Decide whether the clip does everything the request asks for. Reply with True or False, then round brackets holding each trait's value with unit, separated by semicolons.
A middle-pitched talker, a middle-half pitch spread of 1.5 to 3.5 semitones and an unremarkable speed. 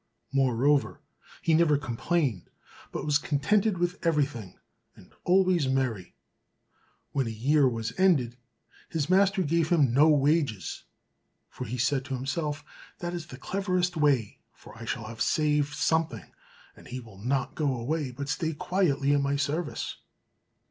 False (145 Hz; 4.4 semitones; 145 wpm)